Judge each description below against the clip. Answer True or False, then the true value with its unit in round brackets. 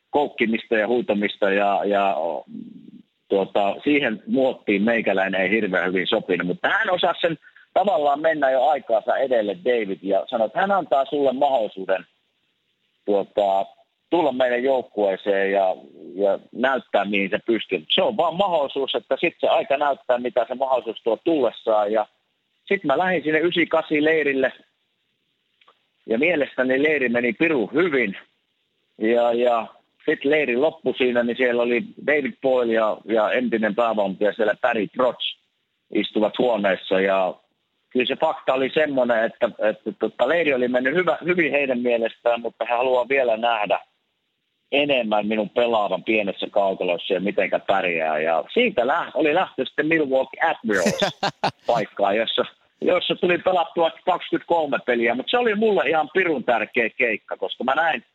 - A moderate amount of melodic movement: False (6.3 semitones)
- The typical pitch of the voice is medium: False (125 Hz)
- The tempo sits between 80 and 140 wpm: False (150 wpm)